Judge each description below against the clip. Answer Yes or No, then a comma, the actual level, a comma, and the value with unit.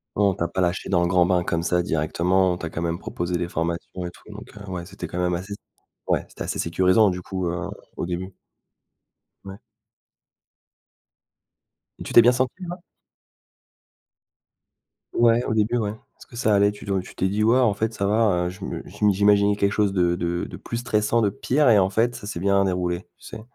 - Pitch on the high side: No, very low, 95 Hz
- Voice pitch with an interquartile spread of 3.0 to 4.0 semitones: Yes, average, 3.3 semitones